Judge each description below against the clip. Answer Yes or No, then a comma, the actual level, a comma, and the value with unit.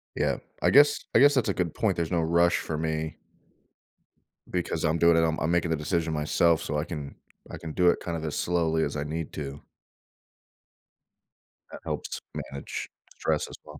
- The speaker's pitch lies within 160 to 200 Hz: No, very low, 80 Hz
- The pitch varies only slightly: Yes, narrow, 1.7 semitones